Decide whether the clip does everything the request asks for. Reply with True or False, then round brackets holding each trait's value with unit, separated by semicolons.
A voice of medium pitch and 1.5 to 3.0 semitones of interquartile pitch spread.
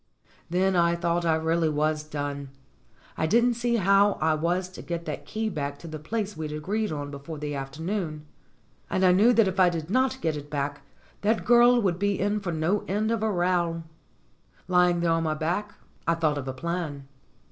False (170 Hz; 4.7 semitones)